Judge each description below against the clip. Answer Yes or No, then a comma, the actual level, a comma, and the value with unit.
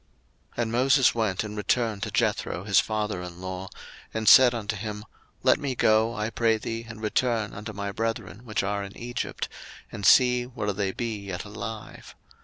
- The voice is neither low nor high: No, low, 110 Hz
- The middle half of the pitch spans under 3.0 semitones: Yes, narrow, 2.5 semitones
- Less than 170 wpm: No, average, 185 wpm